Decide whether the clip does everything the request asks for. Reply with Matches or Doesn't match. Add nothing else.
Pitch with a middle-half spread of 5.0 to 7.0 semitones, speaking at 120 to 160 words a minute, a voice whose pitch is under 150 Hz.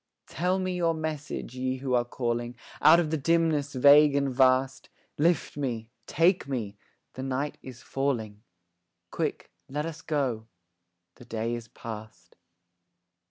Doesn't match